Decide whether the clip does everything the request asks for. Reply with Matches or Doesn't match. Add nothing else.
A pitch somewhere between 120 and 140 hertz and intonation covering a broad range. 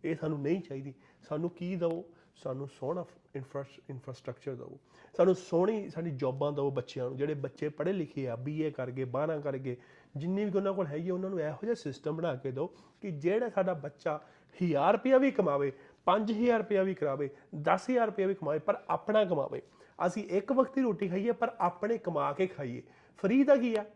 Doesn't match